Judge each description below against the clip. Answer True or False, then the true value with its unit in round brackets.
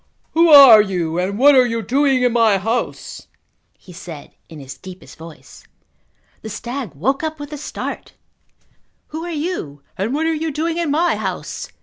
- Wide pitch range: True (8.2 semitones)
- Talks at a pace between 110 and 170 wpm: False (180 wpm)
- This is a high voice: True (245 Hz)